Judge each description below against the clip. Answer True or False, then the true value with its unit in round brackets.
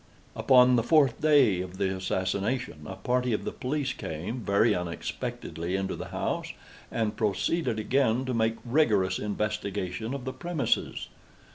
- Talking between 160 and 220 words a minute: False (145 wpm)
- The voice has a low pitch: True (110 Hz)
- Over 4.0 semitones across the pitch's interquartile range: True (5.2 semitones)